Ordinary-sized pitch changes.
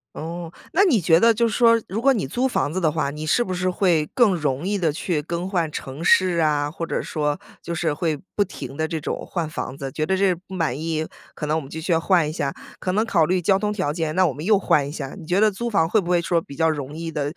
Yes: average, 3.8 semitones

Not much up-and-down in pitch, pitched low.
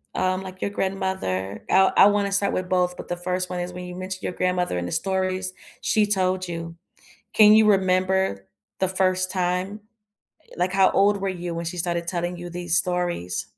No: narrow, 1.3 semitones; medium, 185 Hz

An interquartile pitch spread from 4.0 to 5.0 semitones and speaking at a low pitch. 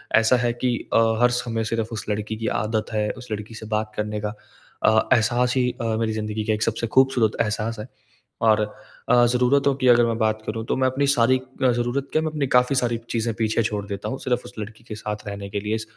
No: narrow, 2.5 semitones; low, 115 Hz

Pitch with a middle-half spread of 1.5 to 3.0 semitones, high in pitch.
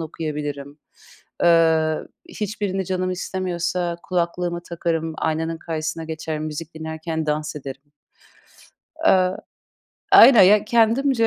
No: average, 2.7 semitones; medium, 165 Hz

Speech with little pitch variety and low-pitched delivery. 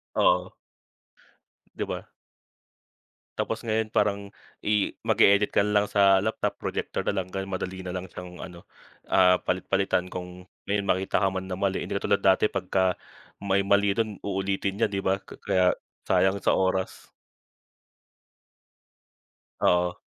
Yes: narrow, 1.4 semitones; very low, 95 Hz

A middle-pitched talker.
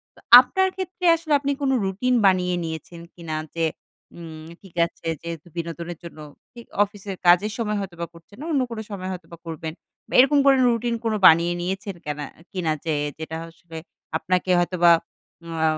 Yes: medium, 180 Hz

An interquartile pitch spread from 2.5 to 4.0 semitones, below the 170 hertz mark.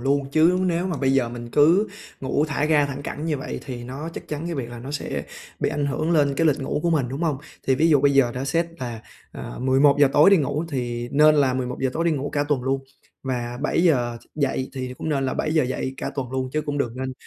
Yes: average, 2.8 semitones; medium, 140 Hz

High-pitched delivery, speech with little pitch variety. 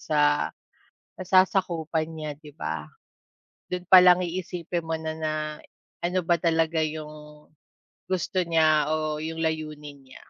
No: medium, 160 Hz; narrow, 2.2 semitones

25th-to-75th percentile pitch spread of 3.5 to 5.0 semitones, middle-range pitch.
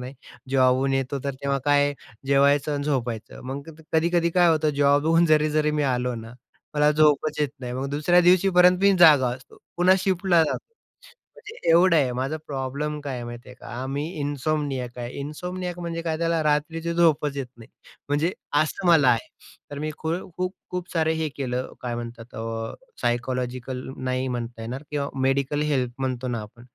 Yes: average, 4.1 semitones; medium, 145 Hz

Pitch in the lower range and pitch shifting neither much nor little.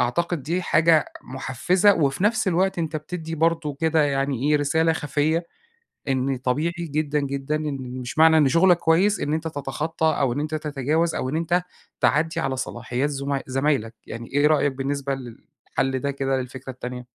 No: medium, 145 Hz; average, 3.3 semitones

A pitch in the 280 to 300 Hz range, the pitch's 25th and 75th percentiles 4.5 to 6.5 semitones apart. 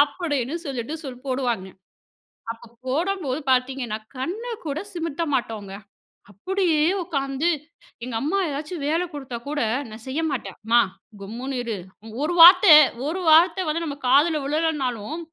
Yes: very high, 285 Hz; average, 4.8 semitones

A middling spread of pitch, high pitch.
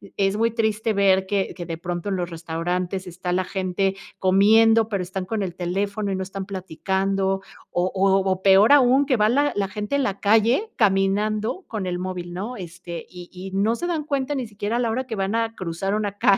Yes: average, 3.0 semitones; high, 195 Hz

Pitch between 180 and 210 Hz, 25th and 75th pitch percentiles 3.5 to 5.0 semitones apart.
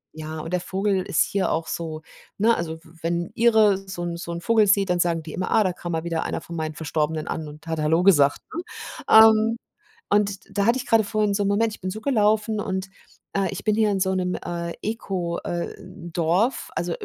Yes: medium, 185 Hz; average, 3.9 semitones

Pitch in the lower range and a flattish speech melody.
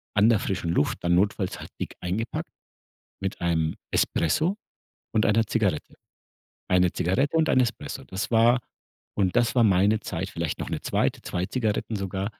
No: low, 100 Hz; average, 4.1 semitones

